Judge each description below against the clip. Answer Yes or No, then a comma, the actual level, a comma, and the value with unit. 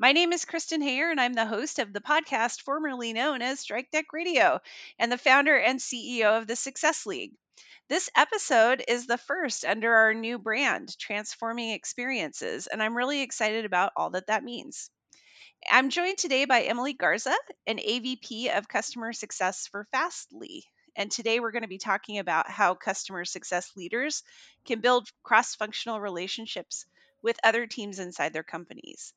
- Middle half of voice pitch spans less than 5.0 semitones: Yes, average, 4.6 semitones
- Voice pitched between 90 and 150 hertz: No, high, 240 Hz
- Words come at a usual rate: Yes, average, 170 wpm